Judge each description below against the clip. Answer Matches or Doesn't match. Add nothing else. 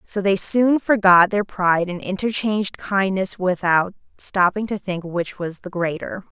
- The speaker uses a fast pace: Doesn't match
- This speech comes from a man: Doesn't match